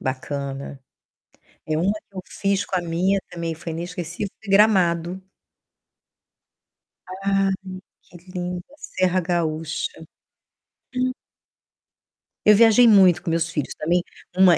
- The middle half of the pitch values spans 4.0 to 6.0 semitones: No, average, 3.0 semitones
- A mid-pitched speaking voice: Yes, medium, 180 Hz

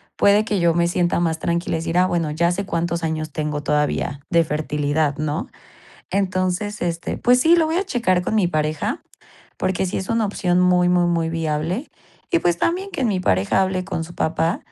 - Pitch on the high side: No, medium, 175 Hz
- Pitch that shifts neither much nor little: Yes, average, 3.2 semitones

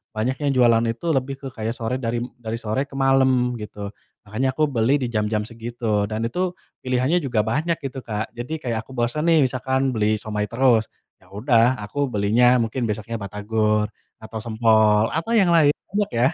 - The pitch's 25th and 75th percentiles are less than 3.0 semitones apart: No, average, 3.4 semitones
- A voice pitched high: No, low, 120 Hz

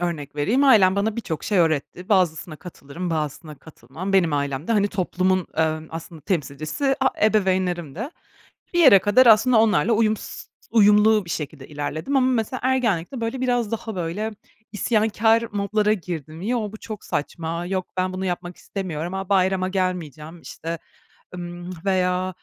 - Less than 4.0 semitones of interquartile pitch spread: No, average, 4.7 semitones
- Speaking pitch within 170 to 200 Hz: Yes, medium, 185 Hz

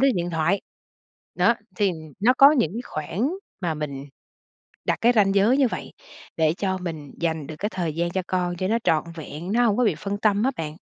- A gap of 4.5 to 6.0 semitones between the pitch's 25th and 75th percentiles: Yes, average, 5.1 semitones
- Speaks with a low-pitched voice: No, medium, 185 Hz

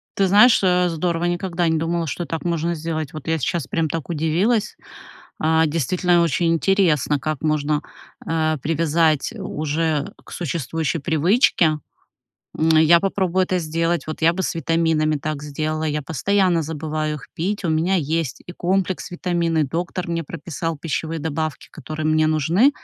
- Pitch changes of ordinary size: No, narrow, 2.1 semitones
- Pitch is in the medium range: Yes, medium, 165 Hz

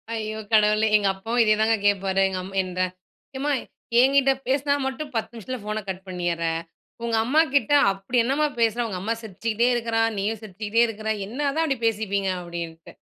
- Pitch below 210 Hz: No, high, 220 Hz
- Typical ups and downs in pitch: Yes, average, 4.1 semitones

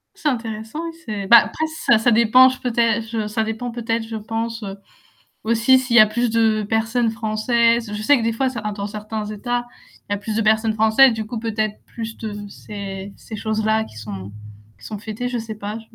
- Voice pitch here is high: Yes, high, 220 Hz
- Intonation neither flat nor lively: No, narrow, 1.5 semitones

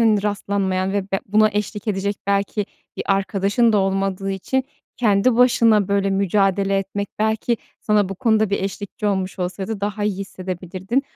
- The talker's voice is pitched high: Yes, high, 200 Hz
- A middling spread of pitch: No, narrow, 1.6 semitones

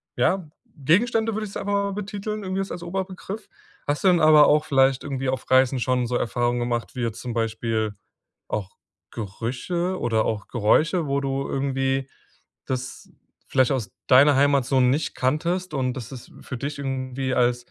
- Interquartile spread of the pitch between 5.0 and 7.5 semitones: Yes, wide, 5.6 semitones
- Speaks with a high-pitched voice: No, low, 135 Hz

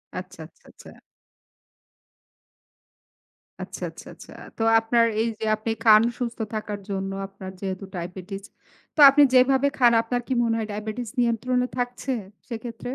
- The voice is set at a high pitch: Yes, high, 225 Hz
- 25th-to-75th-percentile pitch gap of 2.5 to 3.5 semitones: Yes, average, 3.0 semitones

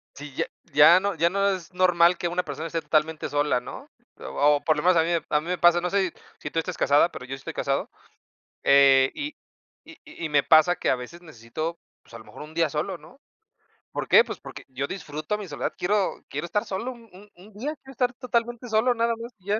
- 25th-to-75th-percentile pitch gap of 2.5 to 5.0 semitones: No, wide, 5.6 semitones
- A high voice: No, medium, 175 Hz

